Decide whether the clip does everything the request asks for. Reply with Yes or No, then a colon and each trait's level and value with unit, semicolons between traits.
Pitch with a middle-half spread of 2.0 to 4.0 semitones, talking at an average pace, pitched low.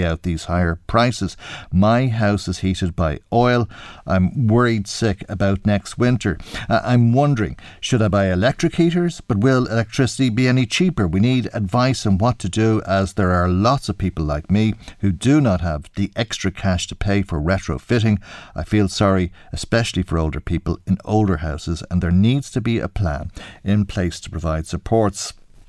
No: average, 4.4 semitones; average, 180 wpm; low, 100 Hz